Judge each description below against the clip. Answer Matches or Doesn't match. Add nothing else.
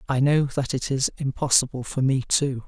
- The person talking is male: Matches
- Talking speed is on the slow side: Doesn't match